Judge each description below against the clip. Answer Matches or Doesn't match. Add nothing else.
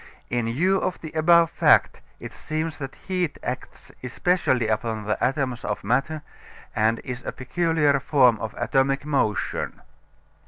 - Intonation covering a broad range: Doesn't match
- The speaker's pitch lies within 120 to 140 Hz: Matches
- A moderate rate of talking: Matches